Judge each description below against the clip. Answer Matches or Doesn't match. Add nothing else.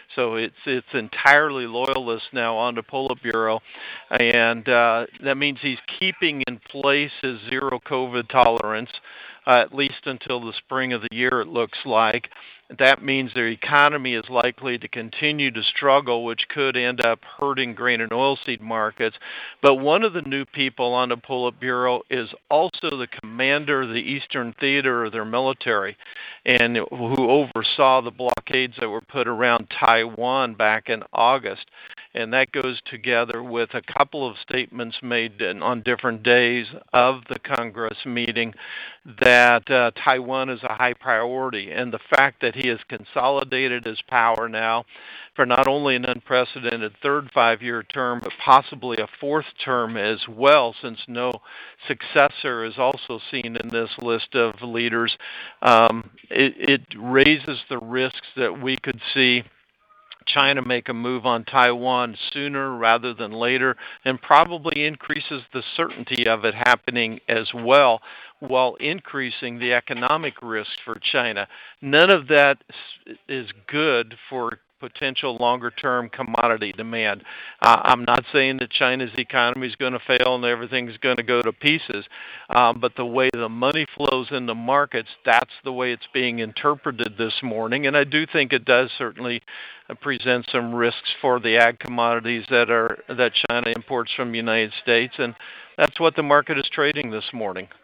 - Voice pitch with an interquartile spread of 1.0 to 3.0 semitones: Matches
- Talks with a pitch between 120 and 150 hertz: Matches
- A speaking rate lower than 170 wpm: Matches